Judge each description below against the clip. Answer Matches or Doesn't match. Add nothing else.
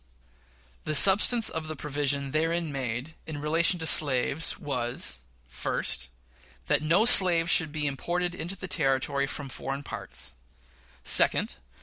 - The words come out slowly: Matches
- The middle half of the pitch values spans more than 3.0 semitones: Matches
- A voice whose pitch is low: Doesn't match